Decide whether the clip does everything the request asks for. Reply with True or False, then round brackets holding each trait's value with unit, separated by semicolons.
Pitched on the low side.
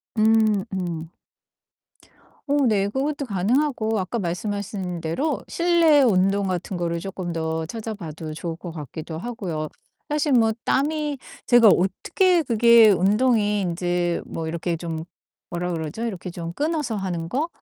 False (195 Hz)